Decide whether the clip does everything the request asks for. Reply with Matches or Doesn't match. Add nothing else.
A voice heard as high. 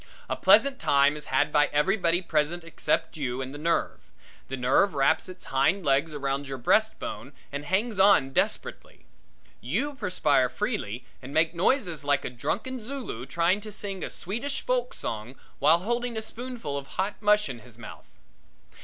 Doesn't match